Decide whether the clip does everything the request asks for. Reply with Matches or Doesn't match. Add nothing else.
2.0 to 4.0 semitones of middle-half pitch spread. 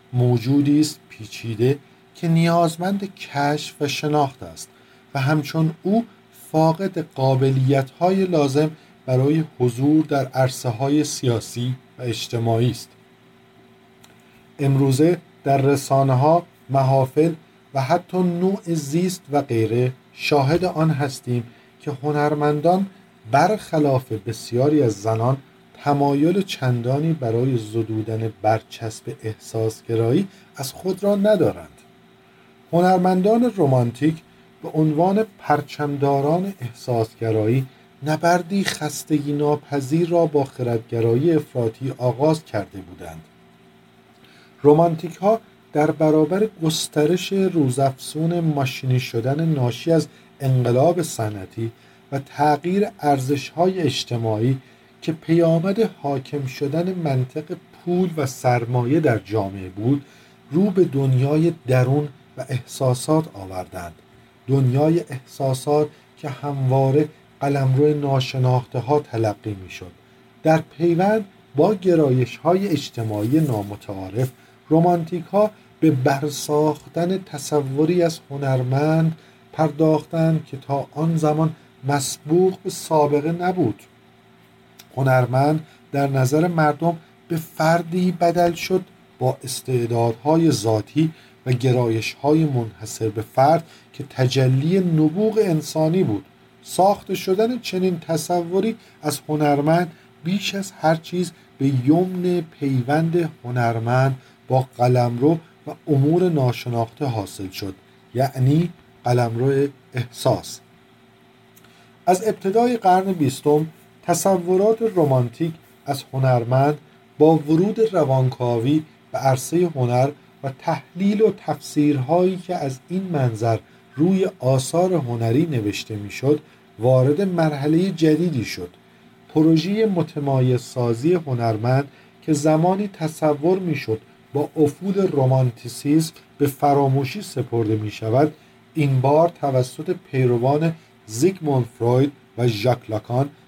Doesn't match